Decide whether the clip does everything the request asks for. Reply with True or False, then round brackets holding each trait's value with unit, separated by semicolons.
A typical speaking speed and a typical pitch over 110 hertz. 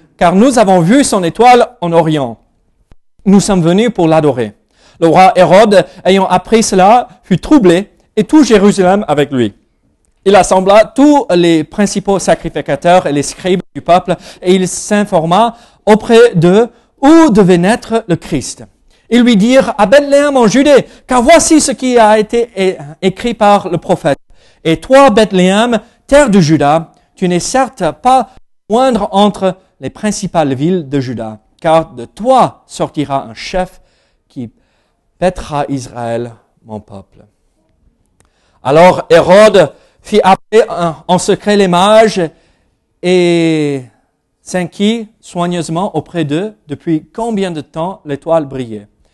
False (135 wpm; 185 Hz)